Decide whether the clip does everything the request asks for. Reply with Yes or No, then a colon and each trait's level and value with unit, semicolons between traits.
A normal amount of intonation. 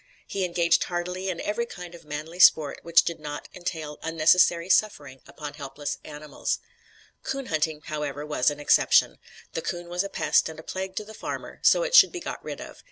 Yes: average, 3.4 semitones